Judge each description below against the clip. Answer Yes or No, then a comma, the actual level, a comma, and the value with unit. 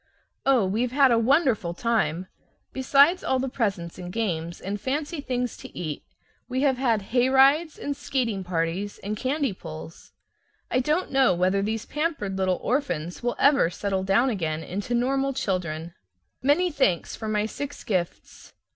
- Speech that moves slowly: No, average, 155 wpm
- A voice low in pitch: No, high, 230 Hz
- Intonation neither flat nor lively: No, wide, 6.5 semitones